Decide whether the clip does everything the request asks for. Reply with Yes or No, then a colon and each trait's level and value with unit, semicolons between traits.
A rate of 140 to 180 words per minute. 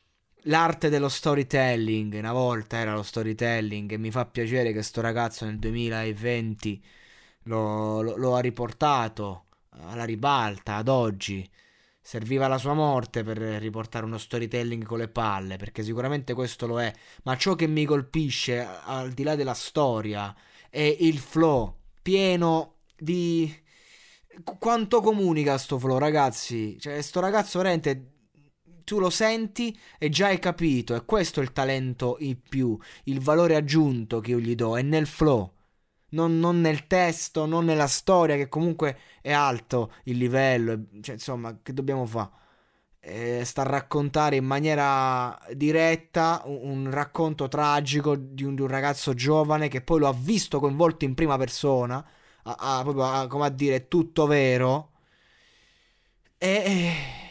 Yes: average, 150 wpm